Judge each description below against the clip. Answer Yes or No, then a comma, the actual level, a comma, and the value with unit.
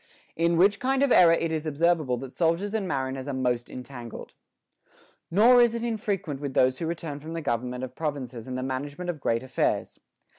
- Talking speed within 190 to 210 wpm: Yes, average, 195 wpm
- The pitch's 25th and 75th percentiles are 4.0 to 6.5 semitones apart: Yes, average, 5.3 semitones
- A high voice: No, medium, 150 Hz